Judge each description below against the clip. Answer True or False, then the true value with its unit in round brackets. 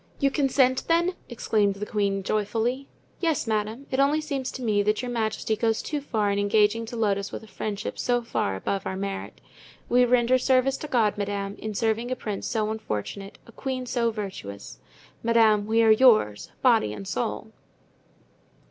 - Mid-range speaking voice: False (220 Hz)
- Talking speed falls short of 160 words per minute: False (180 wpm)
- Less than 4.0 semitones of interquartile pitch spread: True (3.6 semitones)